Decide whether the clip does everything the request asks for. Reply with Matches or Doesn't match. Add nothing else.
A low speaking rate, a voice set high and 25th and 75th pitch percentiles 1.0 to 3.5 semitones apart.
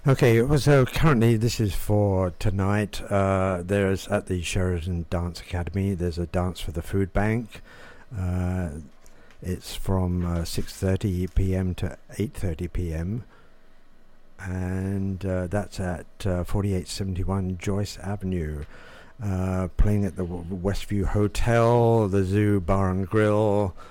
Doesn't match